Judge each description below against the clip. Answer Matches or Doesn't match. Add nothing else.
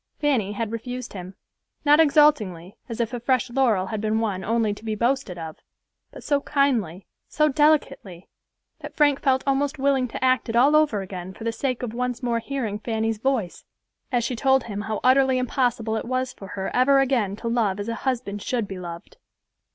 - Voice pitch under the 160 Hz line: Doesn't match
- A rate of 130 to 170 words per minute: Doesn't match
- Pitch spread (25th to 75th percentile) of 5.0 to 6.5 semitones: Doesn't match